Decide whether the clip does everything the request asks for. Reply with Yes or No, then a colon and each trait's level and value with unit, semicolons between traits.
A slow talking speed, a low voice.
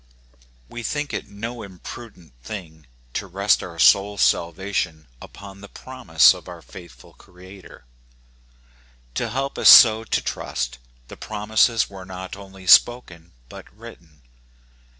Yes: slow, 130 wpm; very low, 95 Hz